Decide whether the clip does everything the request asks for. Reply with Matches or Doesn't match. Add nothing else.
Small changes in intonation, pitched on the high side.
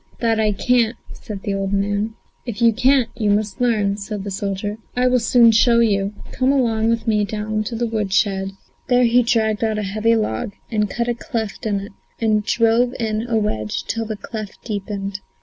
Matches